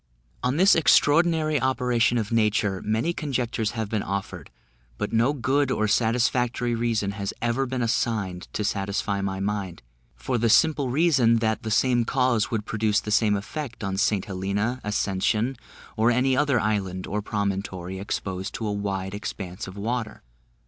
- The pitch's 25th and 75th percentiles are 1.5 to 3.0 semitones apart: No, average, 3.7 semitones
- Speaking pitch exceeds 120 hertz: No, low, 110 Hz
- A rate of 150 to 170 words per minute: Yes, average, 160 wpm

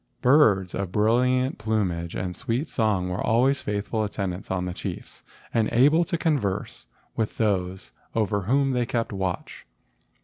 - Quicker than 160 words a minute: No, average, 145 wpm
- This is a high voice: No, low, 110 Hz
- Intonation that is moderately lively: Yes, average, 4.9 semitones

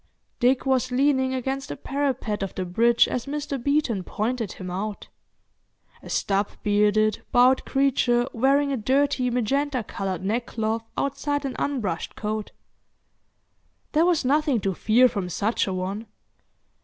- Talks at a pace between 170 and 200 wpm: No, slow, 135 wpm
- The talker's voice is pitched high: Yes, high, 245 Hz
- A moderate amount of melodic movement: Yes, average, 4.5 semitones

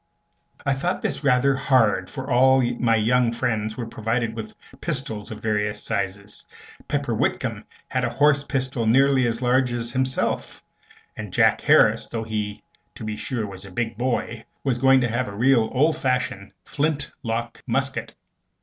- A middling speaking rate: Yes, average, 160 wpm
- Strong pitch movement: No, average, 3.1 semitones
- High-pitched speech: No, low, 120 Hz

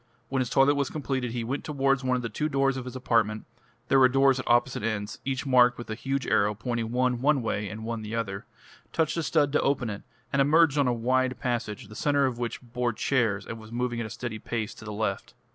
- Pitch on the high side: No, low, 125 Hz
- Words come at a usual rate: No, fast, 245 wpm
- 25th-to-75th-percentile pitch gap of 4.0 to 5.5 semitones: No, average, 3.1 semitones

